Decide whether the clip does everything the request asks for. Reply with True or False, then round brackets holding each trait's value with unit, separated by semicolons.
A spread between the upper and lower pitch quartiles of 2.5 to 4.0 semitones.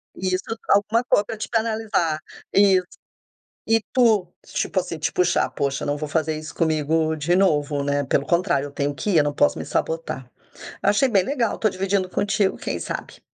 False (5.2 semitones)